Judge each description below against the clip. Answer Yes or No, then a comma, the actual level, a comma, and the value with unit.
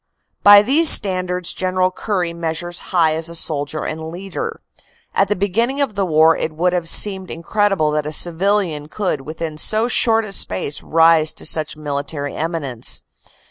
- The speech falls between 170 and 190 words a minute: No, average, 160 wpm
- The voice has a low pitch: No, medium, 170 Hz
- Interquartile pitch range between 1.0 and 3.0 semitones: No, average, 4.0 semitones